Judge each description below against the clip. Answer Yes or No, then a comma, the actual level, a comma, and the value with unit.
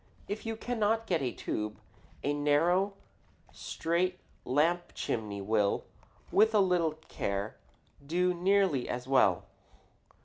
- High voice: No, medium, 170 Hz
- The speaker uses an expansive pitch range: Yes, wide, 7.2 semitones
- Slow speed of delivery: Yes, slow, 115 wpm